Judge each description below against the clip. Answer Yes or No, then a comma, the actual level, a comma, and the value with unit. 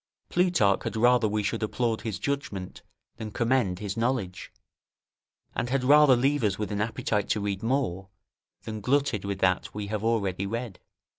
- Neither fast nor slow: Yes, average, 165 wpm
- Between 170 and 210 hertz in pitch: No, low, 110 Hz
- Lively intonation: No, average, 3.9 semitones